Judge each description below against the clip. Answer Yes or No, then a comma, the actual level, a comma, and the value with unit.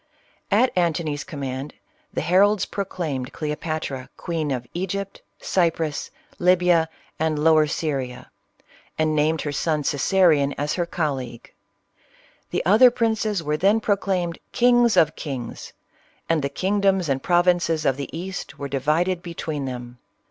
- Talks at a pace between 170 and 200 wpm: No, average, 140 wpm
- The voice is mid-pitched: Yes, medium, 160 Hz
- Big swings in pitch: No, average, 4.2 semitones